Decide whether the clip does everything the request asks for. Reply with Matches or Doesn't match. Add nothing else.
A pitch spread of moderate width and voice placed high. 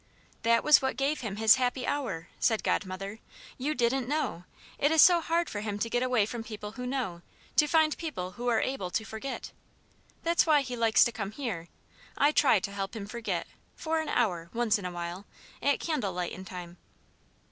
Doesn't match